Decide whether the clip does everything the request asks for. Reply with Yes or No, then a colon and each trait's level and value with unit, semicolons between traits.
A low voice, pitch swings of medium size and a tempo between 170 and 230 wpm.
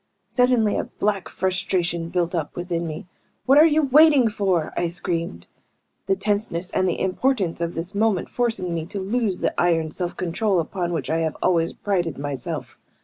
No: medium, 180 Hz; average, 3.9 semitones; average, 175 wpm